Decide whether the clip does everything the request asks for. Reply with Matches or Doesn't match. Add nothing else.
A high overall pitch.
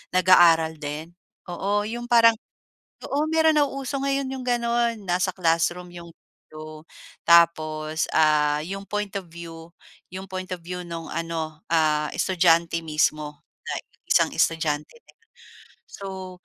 Doesn't match